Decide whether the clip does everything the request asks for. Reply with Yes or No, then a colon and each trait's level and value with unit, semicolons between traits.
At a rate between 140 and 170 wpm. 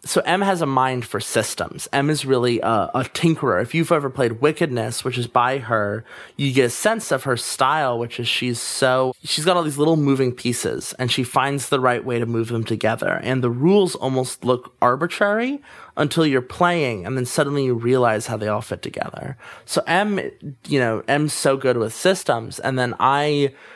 No: fast, 205 wpm